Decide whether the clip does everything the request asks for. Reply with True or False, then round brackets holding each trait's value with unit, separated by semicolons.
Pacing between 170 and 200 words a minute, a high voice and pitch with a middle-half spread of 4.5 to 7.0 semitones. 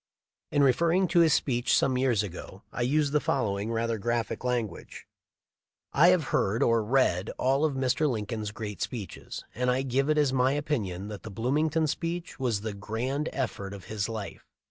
False (180 wpm; 125 Hz; 5.1 semitones)